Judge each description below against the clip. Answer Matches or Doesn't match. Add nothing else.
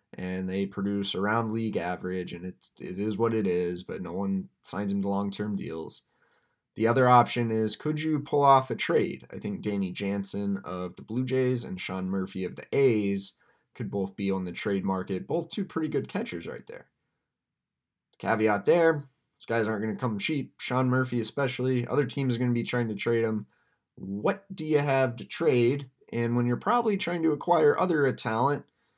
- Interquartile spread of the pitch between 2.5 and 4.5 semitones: Doesn't match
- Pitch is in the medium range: Doesn't match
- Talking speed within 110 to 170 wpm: Doesn't match